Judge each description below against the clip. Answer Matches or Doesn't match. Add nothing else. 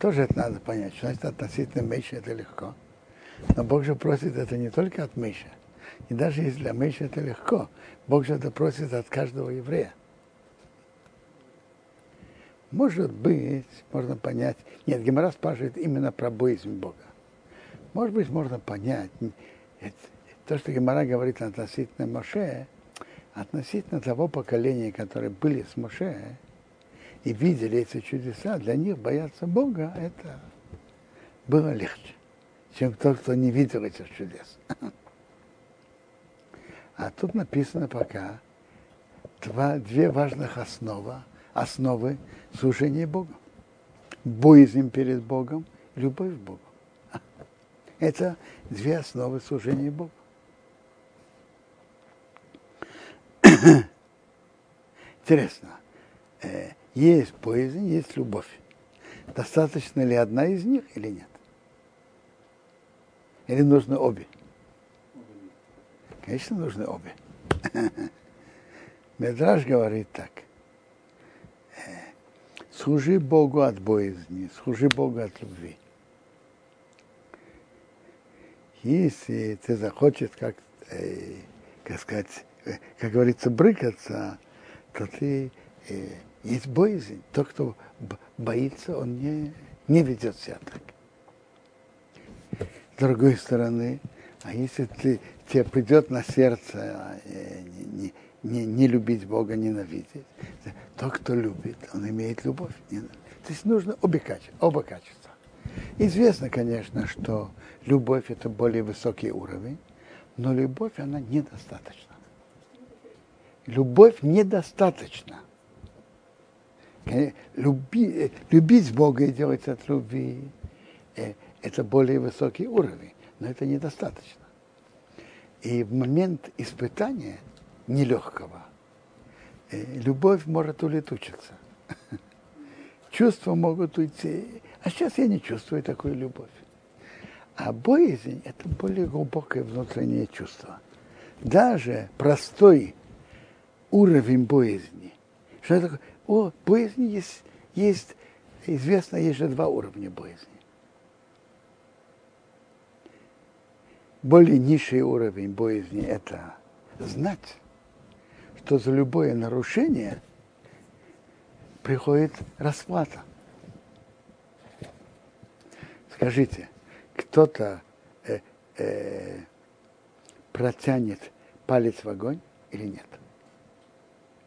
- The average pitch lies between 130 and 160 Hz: Matches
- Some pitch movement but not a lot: Matches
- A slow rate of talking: Matches